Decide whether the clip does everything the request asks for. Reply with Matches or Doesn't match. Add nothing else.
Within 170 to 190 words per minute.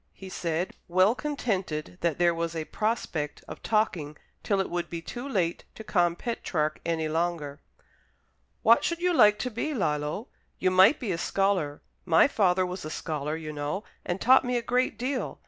Matches